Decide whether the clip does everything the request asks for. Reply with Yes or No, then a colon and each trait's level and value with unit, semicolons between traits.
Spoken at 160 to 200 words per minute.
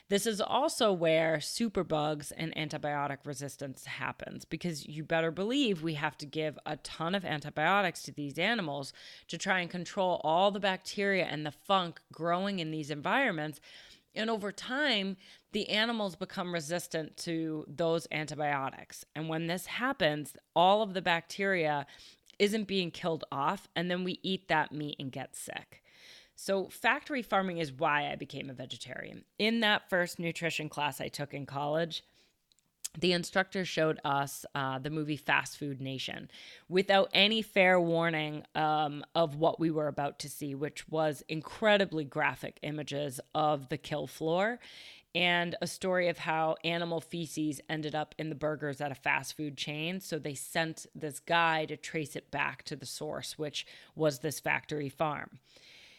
Yes: average, 165 wpm